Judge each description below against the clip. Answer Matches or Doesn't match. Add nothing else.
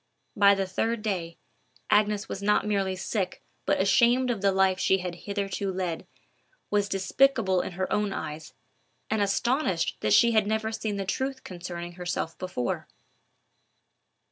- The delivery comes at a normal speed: Matches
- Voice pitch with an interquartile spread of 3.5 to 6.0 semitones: Doesn't match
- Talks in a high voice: Matches